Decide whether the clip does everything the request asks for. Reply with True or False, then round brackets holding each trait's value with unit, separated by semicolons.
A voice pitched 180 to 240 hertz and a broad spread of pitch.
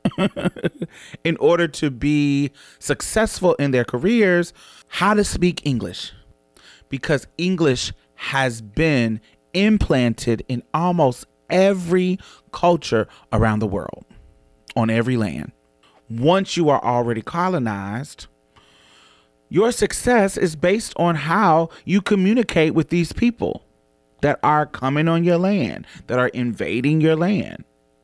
False (150 Hz; 7.5 semitones)